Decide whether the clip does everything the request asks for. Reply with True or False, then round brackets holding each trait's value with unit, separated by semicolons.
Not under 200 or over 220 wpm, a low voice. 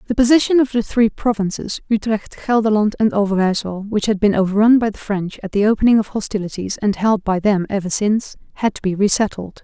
False (205 wpm; 210 Hz)